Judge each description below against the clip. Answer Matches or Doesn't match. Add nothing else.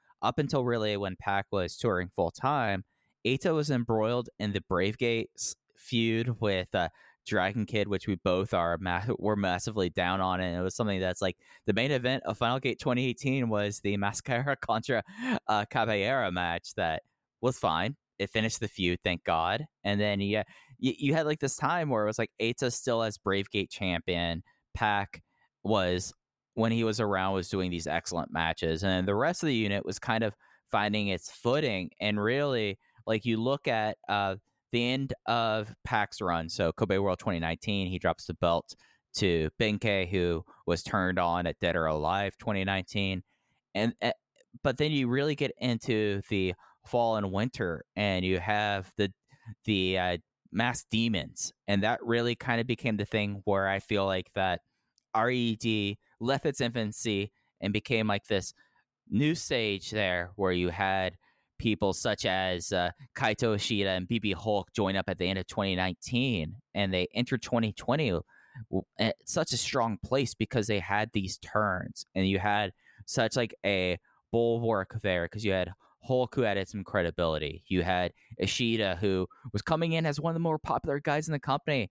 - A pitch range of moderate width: Matches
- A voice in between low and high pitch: Doesn't match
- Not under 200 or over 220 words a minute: Doesn't match